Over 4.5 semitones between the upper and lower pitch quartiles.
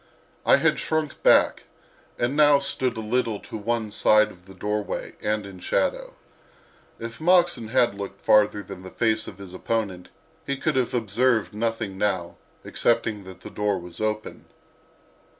No: average, 3.6 semitones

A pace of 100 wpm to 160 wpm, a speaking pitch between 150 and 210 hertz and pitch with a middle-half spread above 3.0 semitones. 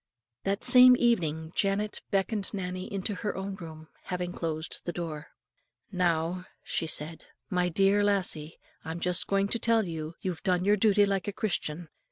No: average, 170 wpm; medium, 185 Hz; average, 3.5 semitones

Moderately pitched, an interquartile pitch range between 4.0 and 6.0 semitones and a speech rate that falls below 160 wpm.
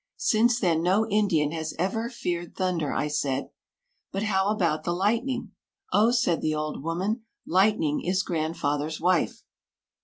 Yes: medium, 180 Hz; average, 5.1 semitones; average, 145 wpm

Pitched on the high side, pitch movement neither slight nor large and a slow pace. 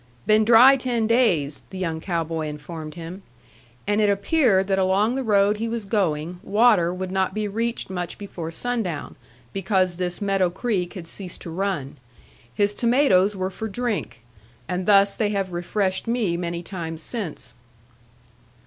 No: high, 195 Hz; average, 3.7 semitones; average, 160 wpm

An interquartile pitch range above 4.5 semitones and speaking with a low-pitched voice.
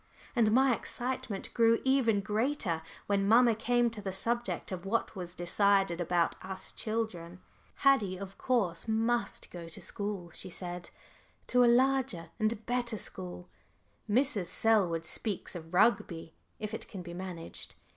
No: average, 5.0 semitones; high, 205 Hz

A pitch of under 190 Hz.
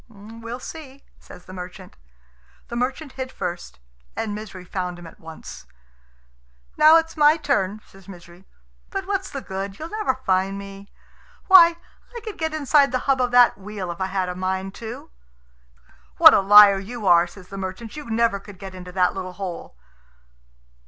No: high, 200 Hz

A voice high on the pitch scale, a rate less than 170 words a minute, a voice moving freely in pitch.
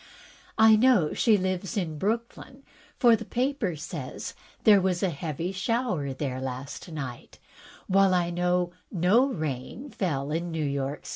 No: medium, 180 Hz; average, 145 wpm; wide, 6.2 semitones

